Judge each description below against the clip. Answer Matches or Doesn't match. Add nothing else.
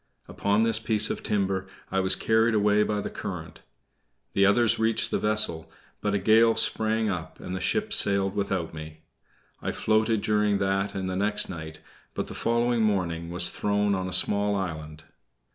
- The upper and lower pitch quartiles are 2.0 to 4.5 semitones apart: Matches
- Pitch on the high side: Doesn't match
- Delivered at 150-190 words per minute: Matches